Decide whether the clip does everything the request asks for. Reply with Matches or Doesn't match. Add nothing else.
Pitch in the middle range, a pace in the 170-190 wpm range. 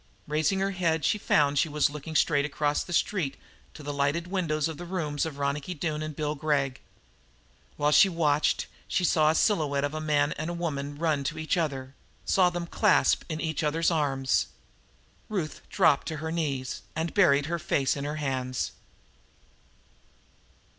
Matches